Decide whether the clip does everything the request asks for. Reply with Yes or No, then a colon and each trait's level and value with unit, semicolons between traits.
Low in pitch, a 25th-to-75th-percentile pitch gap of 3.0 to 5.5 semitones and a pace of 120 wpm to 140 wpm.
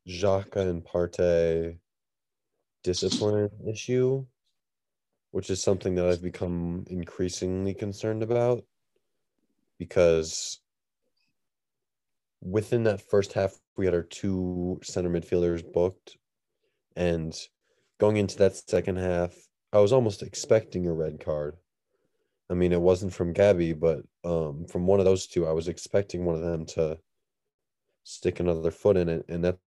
No: very low, 90 Hz; narrow, 2.6 semitones; slow, 135 wpm